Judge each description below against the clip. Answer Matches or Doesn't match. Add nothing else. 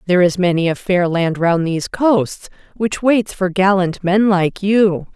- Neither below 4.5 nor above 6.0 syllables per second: Doesn't match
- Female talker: Matches